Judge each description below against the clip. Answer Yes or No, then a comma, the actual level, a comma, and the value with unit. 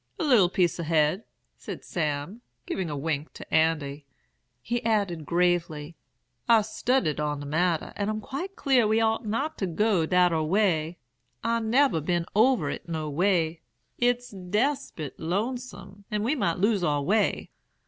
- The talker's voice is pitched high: No, medium, 180 Hz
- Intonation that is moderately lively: No, wide, 5.7 semitones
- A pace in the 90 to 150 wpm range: No, average, 160 wpm